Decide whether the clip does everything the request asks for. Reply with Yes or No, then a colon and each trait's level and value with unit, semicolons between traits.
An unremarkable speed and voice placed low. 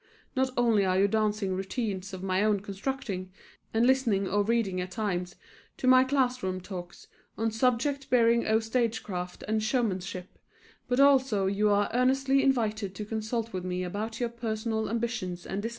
No: average, 170 wpm; high, 220 Hz